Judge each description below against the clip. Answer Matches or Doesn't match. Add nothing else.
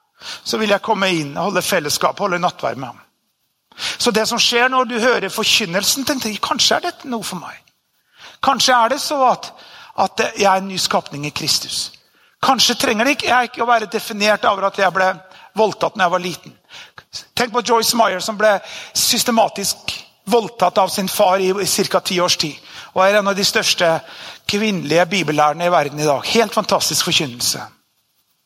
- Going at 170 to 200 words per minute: Matches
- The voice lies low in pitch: Doesn't match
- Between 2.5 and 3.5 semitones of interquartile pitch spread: Doesn't match